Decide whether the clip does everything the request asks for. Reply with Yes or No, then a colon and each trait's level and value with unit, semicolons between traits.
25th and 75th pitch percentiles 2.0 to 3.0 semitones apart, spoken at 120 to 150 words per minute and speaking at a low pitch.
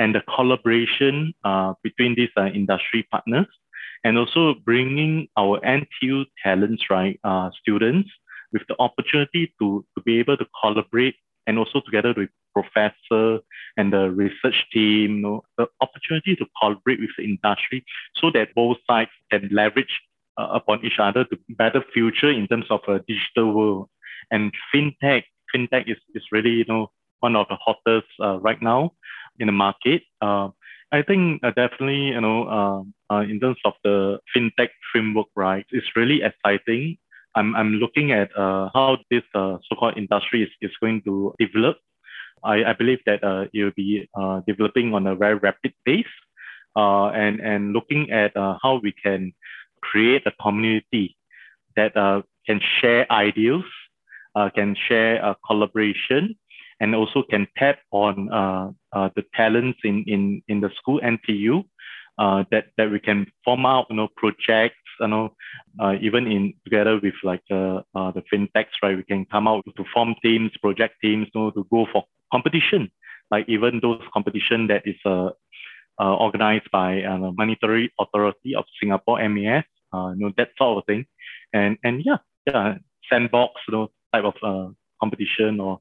No: average, 2.7 semitones; average, 170 wpm; low, 110 Hz